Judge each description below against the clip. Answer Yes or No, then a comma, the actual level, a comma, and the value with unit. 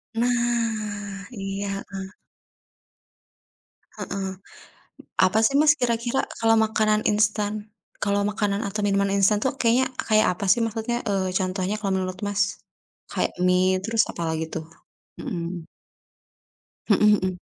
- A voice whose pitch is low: No, high, 205 Hz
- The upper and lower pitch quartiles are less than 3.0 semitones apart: Yes, narrow, 2.5 semitones